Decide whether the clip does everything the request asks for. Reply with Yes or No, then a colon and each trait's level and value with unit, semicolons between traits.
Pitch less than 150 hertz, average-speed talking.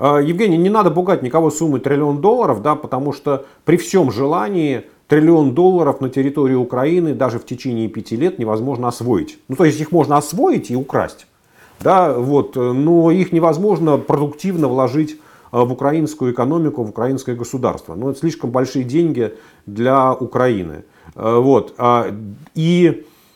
Yes: medium, 140 Hz; average, 145 wpm